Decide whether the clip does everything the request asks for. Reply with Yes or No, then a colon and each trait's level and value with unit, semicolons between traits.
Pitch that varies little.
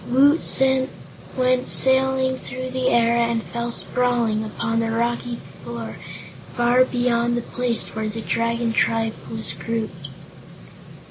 Yes: narrow, 1.8 semitones